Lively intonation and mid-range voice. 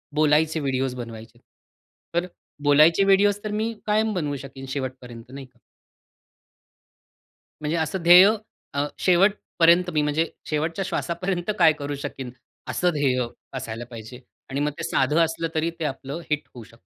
No: average, 4.6 semitones; medium, 150 Hz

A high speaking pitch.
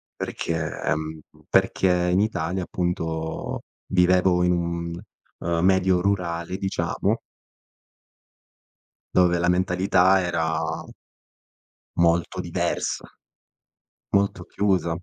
No: very low, 90 Hz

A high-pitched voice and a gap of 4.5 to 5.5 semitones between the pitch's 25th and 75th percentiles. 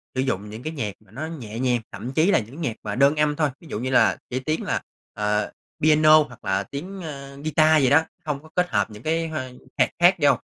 No: medium, 140 Hz; average, 5.1 semitones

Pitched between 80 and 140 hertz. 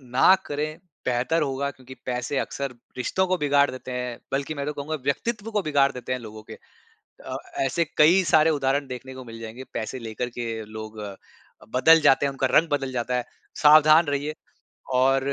Yes: low, 135 Hz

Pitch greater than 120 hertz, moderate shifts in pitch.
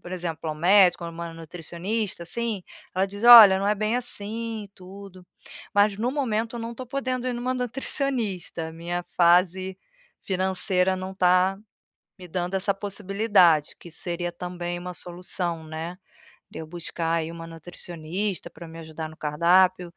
Yes: medium, 185 Hz; average, 3.3 semitones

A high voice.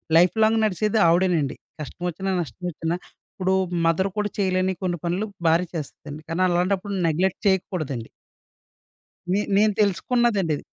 No: medium, 180 Hz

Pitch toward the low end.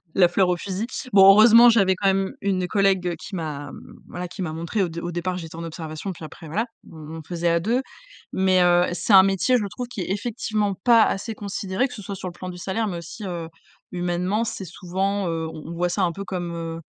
No: medium, 185 Hz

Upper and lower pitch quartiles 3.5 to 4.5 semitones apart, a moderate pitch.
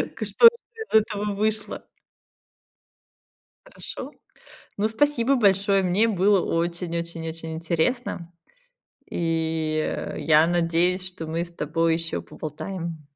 Yes: average, 4.2 semitones; medium, 175 Hz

